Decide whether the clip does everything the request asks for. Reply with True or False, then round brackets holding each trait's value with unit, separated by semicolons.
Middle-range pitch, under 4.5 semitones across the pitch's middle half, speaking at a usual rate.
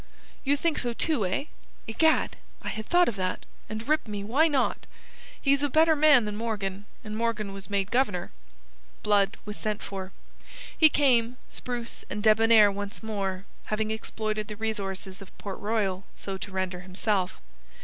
False (215 Hz; 3.4 semitones; 165 wpm)